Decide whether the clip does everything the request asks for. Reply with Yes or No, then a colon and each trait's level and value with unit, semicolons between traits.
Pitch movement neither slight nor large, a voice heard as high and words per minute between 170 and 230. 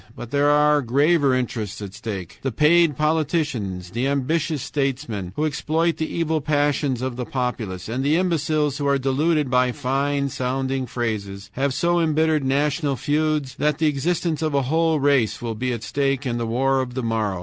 No: average, 3.6 semitones; medium, 140 Hz; average, 185 wpm